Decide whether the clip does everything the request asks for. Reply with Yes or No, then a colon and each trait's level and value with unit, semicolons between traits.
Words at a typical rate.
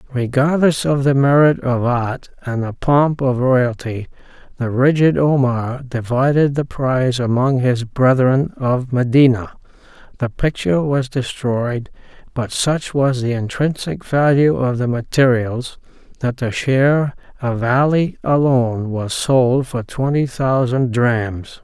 No: slow, 130 wpm